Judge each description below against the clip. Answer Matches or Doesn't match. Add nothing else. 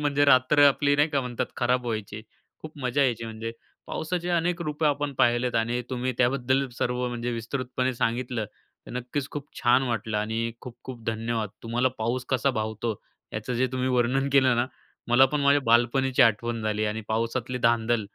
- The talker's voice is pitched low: Matches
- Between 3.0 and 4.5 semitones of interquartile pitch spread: Doesn't match